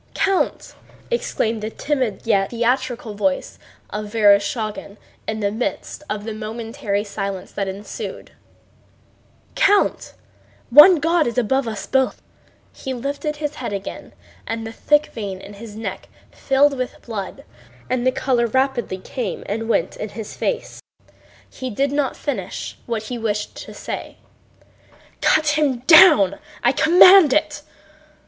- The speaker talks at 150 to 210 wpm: No, average, 140 wpm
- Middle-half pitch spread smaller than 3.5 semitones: No, average, 5.1 semitones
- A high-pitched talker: Yes, high, 235 Hz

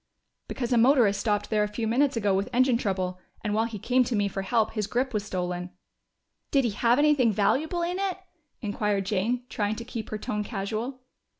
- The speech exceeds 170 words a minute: Yes, fast, 205 wpm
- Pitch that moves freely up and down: No, average, 3.6 semitones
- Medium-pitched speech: No, high, 220 Hz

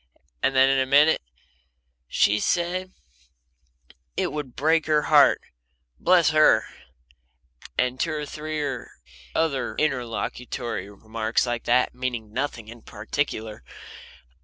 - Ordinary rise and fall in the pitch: Yes, average, 4.7 semitones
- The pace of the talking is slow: Yes, slow, 110 wpm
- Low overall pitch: Yes, low, 130 Hz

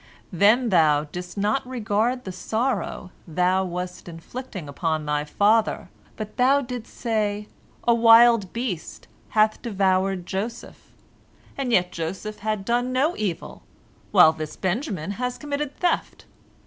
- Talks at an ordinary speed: No, slow, 130 wpm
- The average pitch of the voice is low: No, high, 210 Hz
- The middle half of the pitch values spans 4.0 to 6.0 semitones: Yes, average, 5.0 semitones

